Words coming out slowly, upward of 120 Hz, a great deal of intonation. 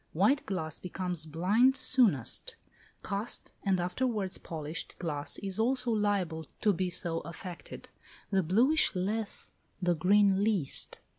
No: slow, 125 wpm; high, 190 Hz; average, 4.1 semitones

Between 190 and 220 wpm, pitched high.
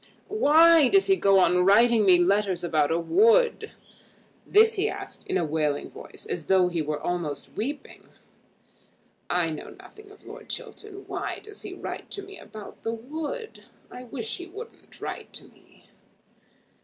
No: average, 165 wpm; high, 230 Hz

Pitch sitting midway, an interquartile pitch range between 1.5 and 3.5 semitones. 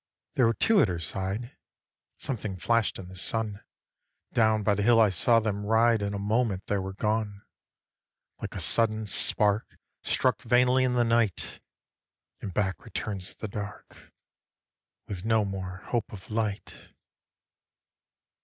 No: low, 105 Hz; average, 2.7 semitones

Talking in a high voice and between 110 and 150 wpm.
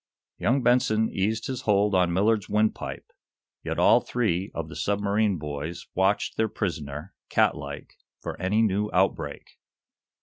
No: low, 100 Hz; average, 145 wpm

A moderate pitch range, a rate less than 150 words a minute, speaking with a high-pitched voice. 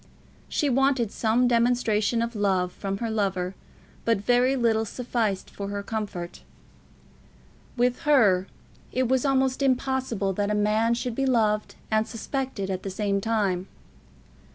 Yes: average, 3.7 semitones; average, 140 wpm; high, 225 Hz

